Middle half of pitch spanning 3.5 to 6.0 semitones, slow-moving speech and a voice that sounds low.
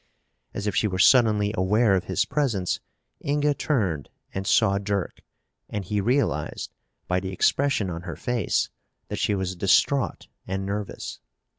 No: average, 4.1 semitones; average, 150 wpm; low, 100 Hz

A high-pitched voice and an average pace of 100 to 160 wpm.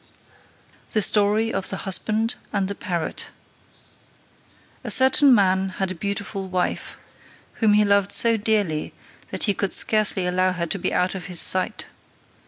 Yes: high, 200 Hz; average, 155 wpm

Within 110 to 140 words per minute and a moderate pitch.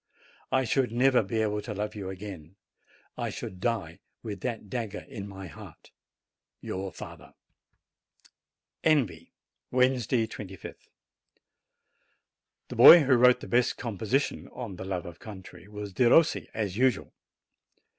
No: slow, 135 wpm; low, 105 Hz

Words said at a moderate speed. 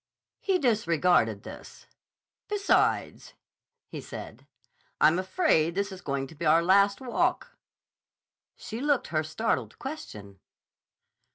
No: slow, 110 wpm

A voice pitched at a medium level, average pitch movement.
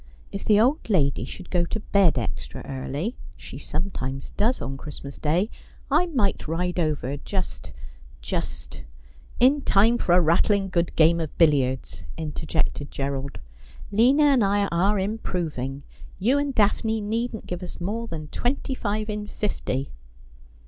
No: medium, 180 Hz; wide, 6.7 semitones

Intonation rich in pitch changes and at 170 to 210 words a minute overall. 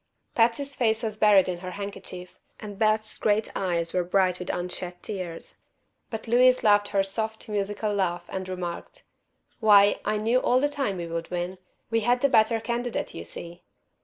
No: average, 3.7 semitones; average, 175 wpm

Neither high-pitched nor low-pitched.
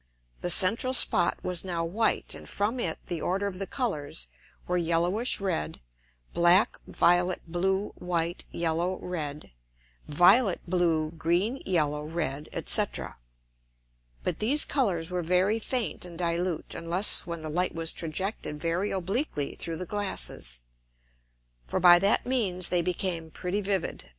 Yes: medium, 175 Hz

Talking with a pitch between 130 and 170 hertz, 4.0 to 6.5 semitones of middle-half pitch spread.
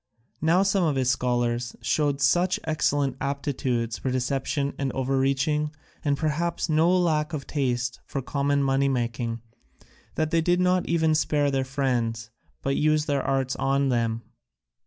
No: medium, 140 Hz; average, 3.1 semitones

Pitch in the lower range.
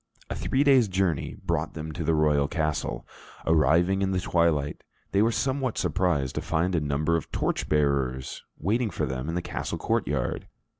Yes: very low, 80 Hz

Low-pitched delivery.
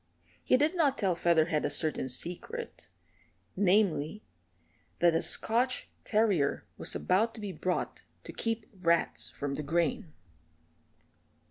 No: medium, 185 Hz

